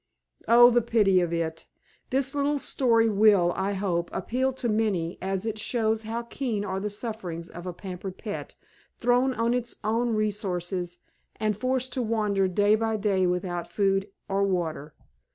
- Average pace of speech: Yes, average, 165 wpm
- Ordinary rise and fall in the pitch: Yes, average, 3.9 semitones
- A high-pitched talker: Yes, high, 210 Hz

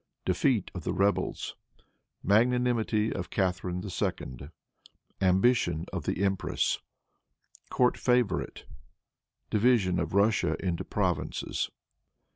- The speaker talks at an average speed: No, slow, 90 wpm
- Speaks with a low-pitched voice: Yes, low, 100 Hz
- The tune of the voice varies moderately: Yes, average, 4.4 semitones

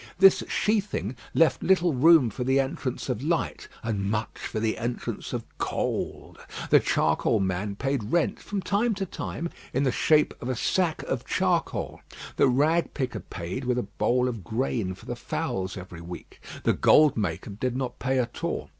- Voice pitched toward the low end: Yes, low, 125 Hz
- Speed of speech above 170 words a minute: Yes, average, 180 wpm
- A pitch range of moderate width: No, wide, 6.7 semitones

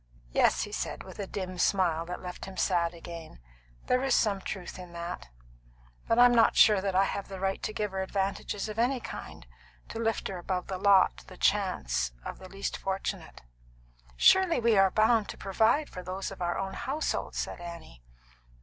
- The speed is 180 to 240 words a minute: Yes, average, 195 wpm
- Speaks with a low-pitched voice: No, high, 190 Hz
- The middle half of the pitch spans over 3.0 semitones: Yes, average, 3.4 semitones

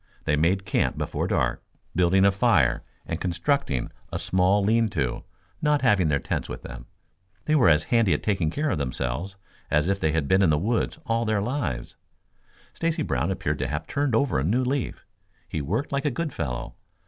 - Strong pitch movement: Yes, wide, 7.9 semitones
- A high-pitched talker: No, very low, 95 Hz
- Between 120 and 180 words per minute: No, average, 200 wpm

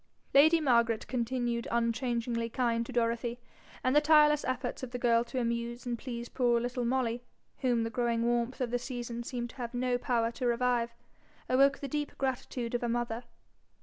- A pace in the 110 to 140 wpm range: No, average, 180 wpm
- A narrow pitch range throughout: Yes, narrow, 1.5 semitones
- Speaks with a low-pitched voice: No, high, 240 Hz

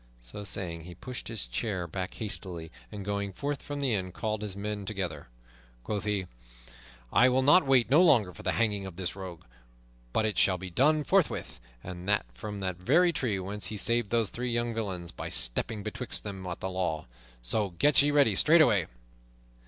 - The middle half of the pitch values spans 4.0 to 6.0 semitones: Yes, average, 4.3 semitones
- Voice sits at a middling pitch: No, low, 100 Hz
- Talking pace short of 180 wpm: No, average, 190 wpm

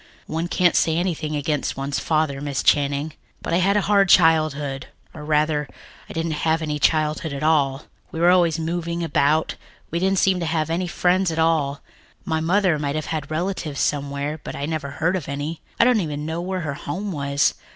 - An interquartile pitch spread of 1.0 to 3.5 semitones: Yes, average, 2.8 semitones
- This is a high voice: No, medium, 160 Hz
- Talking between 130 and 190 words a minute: No, average, 200 wpm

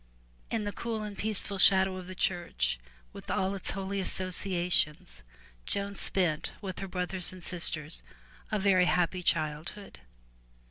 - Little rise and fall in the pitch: Yes, narrow, 2.1 semitones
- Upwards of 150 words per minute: No, average, 140 wpm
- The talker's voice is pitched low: No, medium, 185 Hz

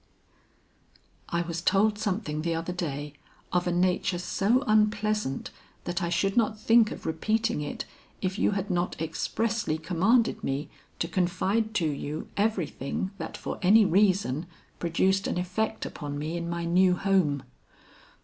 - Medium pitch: Yes, medium, 180 Hz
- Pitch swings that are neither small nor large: Yes, average, 4.1 semitones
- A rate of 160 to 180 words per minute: No, average, 150 wpm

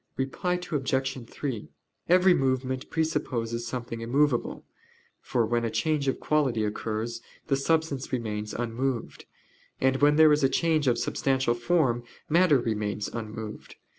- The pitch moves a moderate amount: Yes, average, 4.1 semitones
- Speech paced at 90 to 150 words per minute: Yes, slow, 135 wpm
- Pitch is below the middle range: Yes, low, 130 Hz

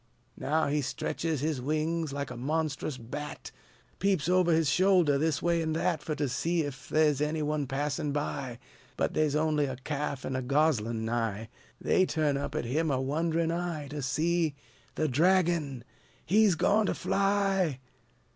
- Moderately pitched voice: Yes, medium, 150 Hz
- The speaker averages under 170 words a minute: No, average, 175 wpm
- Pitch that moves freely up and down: No, average, 3.1 semitones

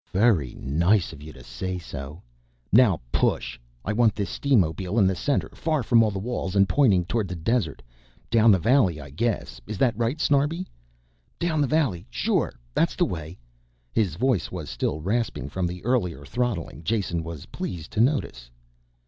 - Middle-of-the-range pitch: No, low, 100 Hz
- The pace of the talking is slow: No, average, 175 wpm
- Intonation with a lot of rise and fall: Yes, wide, 6.5 semitones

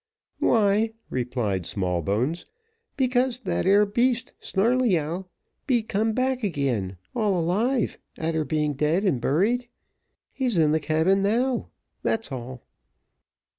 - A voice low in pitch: No, high, 190 Hz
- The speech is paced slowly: Yes, slow, 115 wpm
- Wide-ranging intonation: Yes, wide, 8.1 semitones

